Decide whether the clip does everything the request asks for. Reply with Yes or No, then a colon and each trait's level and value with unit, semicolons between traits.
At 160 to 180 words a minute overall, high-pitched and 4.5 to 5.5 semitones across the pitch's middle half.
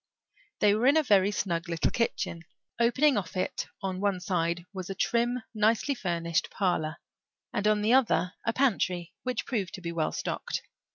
Yes: average, 175 wpm; high, 200 Hz; average, 5.1 semitones